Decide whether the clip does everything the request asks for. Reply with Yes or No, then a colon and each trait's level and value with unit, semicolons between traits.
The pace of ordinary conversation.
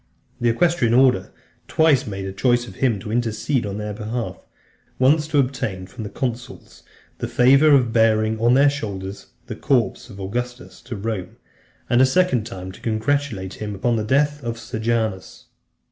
Yes: average, 170 wpm